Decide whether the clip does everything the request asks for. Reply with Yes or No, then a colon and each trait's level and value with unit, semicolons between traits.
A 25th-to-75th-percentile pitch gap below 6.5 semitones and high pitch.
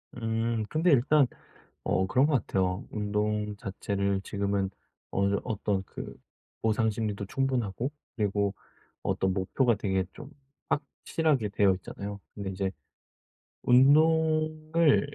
No: average, 5.3 semitones; low, 105 Hz